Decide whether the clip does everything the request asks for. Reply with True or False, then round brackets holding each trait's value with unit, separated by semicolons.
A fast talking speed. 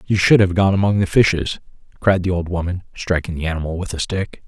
True (230 wpm)